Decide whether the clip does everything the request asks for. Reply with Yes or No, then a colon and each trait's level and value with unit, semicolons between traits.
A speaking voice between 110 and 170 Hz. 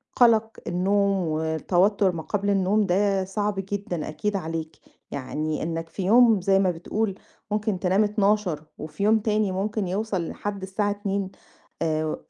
No: high, 195 Hz